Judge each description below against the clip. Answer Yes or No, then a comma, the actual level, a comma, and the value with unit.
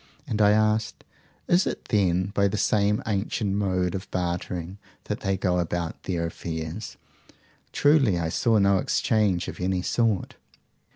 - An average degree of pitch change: Yes, average, 3.1 semitones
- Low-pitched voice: Yes, very low, 95 Hz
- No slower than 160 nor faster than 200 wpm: No, average, 150 wpm